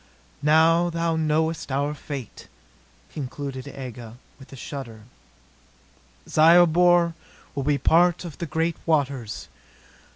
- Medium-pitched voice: Yes, medium, 150 Hz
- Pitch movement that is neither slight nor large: Yes, average, 3.5 semitones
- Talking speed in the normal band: No, slow, 110 wpm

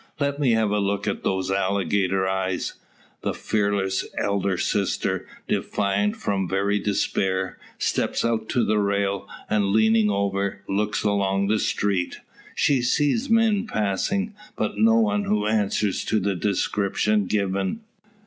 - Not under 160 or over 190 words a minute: No, average, 140 wpm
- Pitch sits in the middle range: No, low, 100 Hz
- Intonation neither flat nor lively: No, narrow, 2.0 semitones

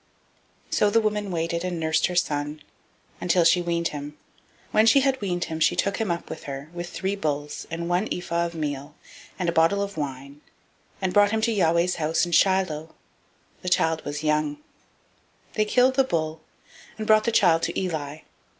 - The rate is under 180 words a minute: No, fast, 205 wpm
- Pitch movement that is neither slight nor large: Yes, average, 4.1 semitones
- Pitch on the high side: No, medium, 170 Hz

